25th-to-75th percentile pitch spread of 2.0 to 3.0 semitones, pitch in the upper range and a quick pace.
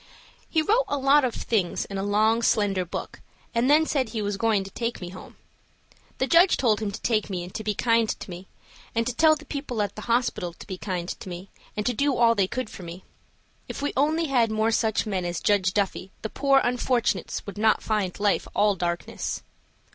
No: average, 4.3 semitones; high, 220 Hz; fast, 225 wpm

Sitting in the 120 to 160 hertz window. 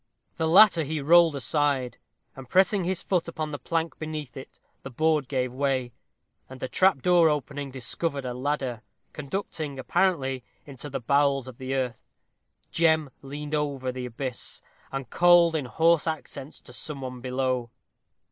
Yes: medium, 140 Hz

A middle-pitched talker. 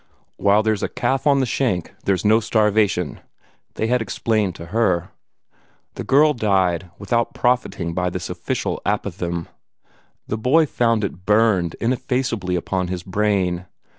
No: low, 105 Hz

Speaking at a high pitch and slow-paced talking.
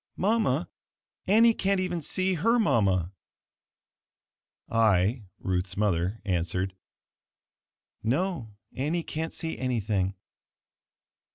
No: low, 115 Hz; slow, 85 wpm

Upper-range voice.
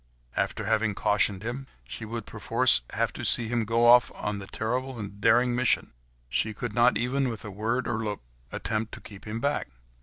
No: low, 115 Hz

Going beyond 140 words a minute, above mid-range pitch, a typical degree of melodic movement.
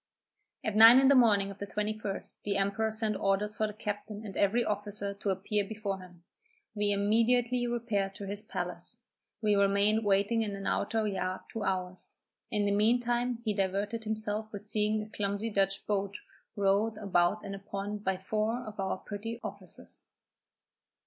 No: average, 175 wpm; high, 205 Hz; narrow, 1.7 semitones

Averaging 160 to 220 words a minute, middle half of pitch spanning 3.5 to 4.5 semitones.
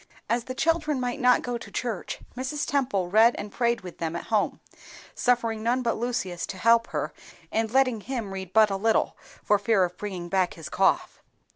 Yes: average, 190 wpm; average, 4.2 semitones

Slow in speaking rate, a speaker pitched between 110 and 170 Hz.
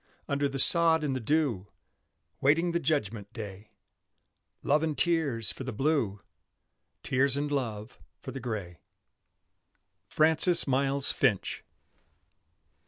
Yes: slow, 115 wpm; low, 135 Hz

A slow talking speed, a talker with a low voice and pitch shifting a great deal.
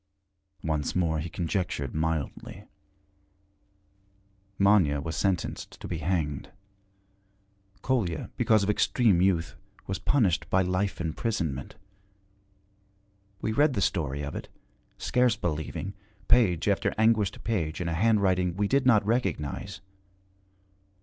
No: slow, 115 wpm; very low, 95 Hz; average, 4.7 semitones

